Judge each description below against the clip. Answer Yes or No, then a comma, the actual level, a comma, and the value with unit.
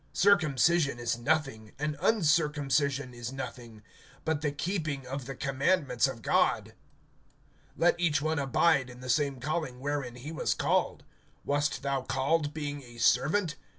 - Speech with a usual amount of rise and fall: Yes, average, 3.3 semitones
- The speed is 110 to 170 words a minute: Yes, average, 145 wpm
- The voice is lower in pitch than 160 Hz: Yes, medium, 140 Hz